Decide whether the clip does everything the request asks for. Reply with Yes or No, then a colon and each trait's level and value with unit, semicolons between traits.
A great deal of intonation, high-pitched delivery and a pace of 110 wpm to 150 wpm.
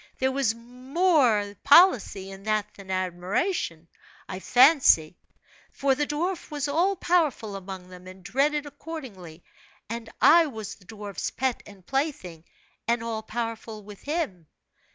Yes: wide, 7.1 semitones; high, 230 Hz; slow, 135 wpm